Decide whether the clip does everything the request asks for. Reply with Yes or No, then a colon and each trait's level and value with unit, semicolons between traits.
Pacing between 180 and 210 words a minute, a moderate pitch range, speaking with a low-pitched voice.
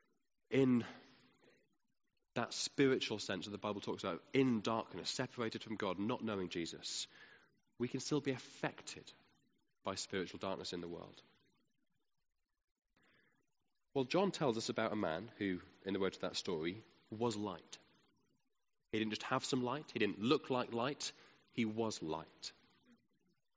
No: average, 150 wpm; average, 3.8 semitones; low, 115 Hz